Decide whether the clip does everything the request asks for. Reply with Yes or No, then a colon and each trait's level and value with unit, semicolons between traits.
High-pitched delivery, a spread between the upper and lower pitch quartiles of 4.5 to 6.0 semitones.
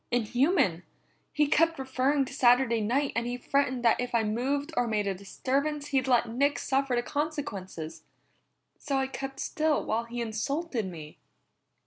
No: very high, 255 Hz; average, 3.7 semitones